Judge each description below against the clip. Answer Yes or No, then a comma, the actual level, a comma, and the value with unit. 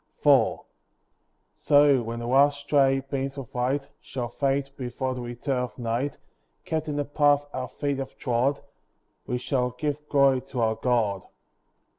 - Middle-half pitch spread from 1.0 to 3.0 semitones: Yes, narrow, 2.4 semitones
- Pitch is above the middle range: No, low, 135 Hz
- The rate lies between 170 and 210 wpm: No, average, 155 wpm